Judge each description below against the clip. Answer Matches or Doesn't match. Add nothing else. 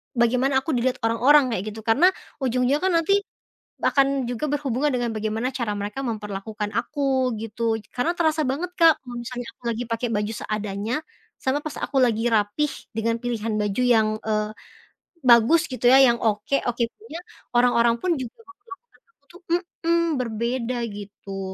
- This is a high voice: Matches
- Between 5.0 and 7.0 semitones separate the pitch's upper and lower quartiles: Doesn't match